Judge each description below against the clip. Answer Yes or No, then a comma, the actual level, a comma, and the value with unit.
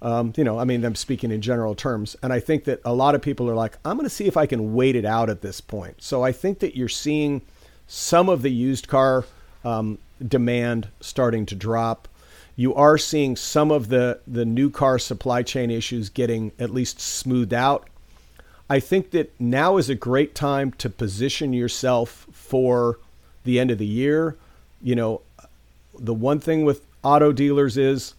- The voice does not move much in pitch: No, average, 3.5 semitones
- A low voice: Yes, low, 125 Hz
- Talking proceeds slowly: No, average, 195 wpm